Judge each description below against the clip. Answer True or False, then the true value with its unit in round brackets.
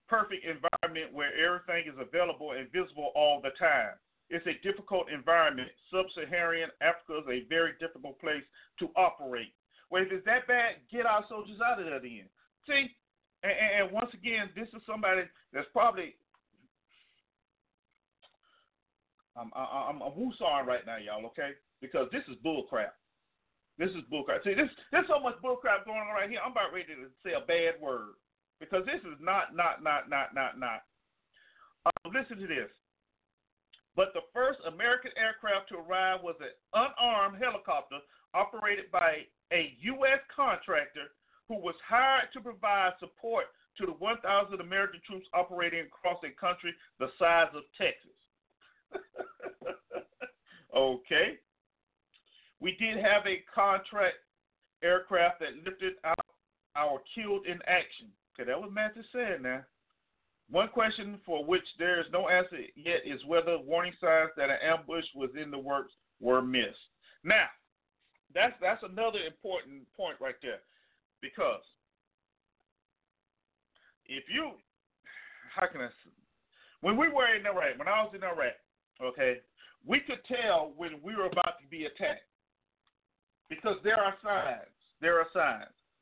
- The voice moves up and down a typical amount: False (5.7 semitones)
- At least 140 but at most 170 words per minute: True (150 wpm)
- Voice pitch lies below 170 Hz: False (185 Hz)